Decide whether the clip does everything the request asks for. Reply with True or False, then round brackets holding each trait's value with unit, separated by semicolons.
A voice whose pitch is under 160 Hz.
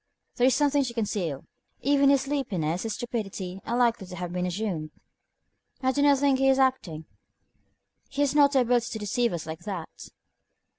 False (235 Hz)